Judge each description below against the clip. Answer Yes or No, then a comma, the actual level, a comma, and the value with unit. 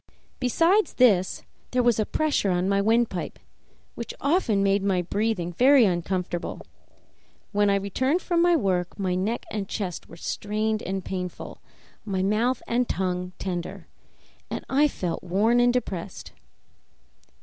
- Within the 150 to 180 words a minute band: No, average, 140 wpm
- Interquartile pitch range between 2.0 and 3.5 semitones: No, average, 4.7 semitones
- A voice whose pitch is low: No, high, 205 Hz